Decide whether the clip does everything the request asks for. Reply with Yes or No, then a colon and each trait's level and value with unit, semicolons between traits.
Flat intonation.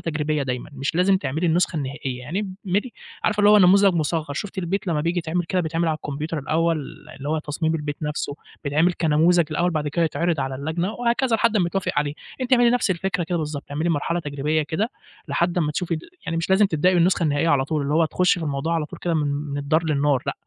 No: average, 3.3 semitones